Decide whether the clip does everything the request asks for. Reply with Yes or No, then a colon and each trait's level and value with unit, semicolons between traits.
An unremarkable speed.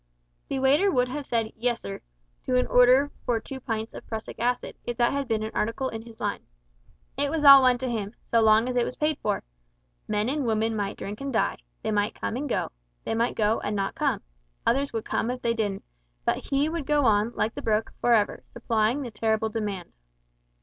No: fast, 220 wpm